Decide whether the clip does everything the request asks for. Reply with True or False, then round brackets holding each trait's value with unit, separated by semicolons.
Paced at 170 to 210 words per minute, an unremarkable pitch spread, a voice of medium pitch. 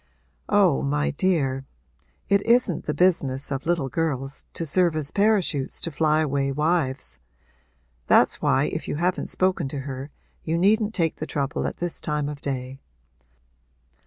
False (155 wpm; 4.4 semitones; 150 Hz)